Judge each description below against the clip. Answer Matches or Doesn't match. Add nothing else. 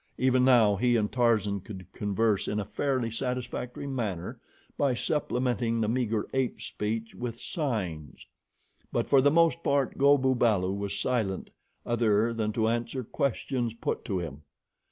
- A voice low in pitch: Matches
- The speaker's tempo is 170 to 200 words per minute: Doesn't match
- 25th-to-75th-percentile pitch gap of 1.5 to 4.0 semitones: Matches